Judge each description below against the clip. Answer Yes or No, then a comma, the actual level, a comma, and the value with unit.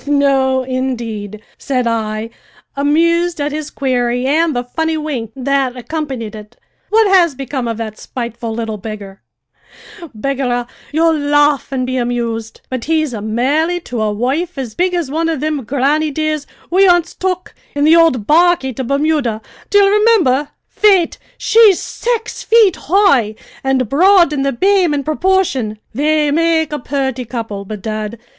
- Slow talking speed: No, average, 150 wpm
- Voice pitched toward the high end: Yes, very high, 275 Hz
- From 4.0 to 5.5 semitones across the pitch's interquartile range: Yes, average, 5.2 semitones